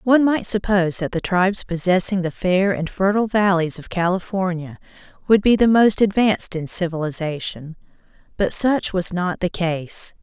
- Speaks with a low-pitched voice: No, medium, 185 Hz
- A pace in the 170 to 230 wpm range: No, average, 160 wpm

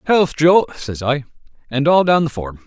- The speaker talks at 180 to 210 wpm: Yes, average, 200 wpm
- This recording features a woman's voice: No, male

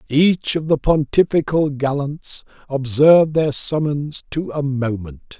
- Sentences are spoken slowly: Yes, slow, 120 wpm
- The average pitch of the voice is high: No, medium, 145 Hz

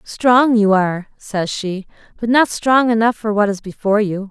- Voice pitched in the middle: No, high, 215 Hz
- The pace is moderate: Yes, average, 195 wpm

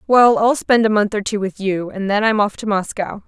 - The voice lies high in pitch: Yes, high, 210 Hz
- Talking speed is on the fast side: Yes, fast, 275 wpm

